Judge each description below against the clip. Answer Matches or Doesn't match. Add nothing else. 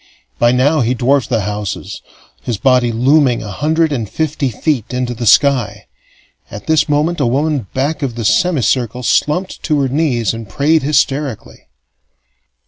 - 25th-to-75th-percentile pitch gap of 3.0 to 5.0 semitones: Matches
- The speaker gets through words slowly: Doesn't match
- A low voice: Matches